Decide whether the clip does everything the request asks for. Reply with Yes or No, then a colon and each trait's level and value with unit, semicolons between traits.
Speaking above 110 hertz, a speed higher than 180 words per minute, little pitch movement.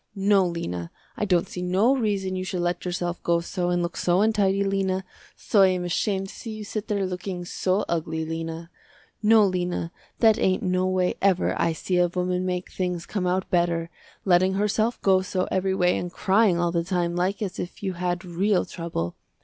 Yes: medium, 185 Hz; average, 200 wpm; narrow, 1.9 semitones